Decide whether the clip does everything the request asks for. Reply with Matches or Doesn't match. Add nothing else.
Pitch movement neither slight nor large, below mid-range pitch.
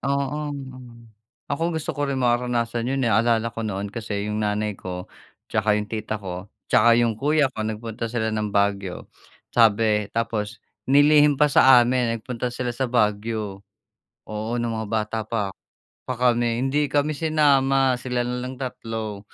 Matches